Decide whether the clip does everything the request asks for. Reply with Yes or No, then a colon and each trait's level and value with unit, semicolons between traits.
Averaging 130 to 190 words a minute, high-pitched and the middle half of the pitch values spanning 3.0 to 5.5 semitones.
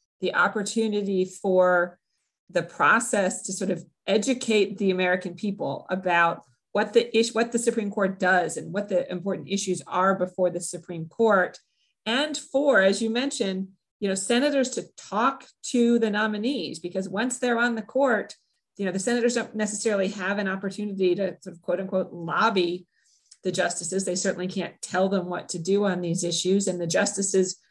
Yes: average, 175 wpm; high, 195 Hz; average, 3.4 semitones